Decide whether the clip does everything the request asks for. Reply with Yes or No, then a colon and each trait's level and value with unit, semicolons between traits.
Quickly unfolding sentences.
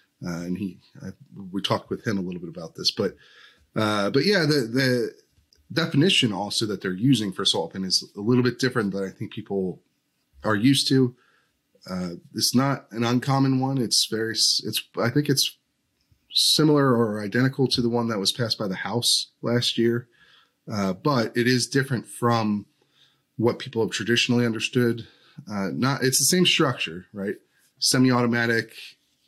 No: average, 170 wpm